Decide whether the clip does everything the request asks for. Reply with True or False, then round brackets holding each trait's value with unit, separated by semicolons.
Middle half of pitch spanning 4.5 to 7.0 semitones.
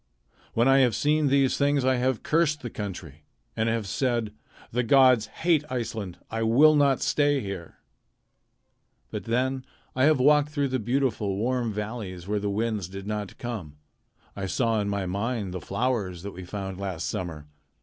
True (4.9 semitones)